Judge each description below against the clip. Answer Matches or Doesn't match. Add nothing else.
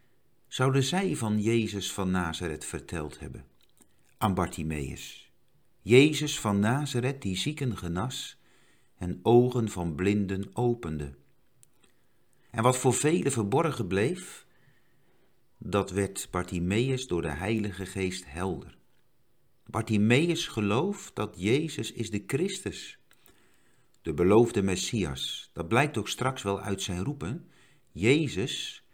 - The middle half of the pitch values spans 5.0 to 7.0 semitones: Matches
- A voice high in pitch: Doesn't match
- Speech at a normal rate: Doesn't match